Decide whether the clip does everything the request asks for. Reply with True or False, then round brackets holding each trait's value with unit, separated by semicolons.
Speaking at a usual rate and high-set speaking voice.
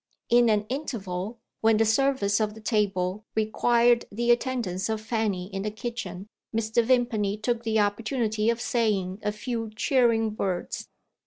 True (150 wpm; 220 Hz)